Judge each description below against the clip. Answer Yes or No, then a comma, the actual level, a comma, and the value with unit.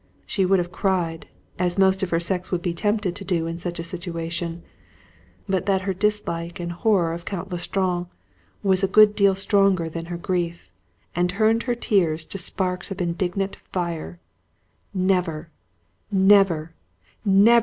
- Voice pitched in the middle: Yes, medium, 180 Hz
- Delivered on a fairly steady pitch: Yes, narrow, 2.3 semitones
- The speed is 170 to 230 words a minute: No, average, 160 wpm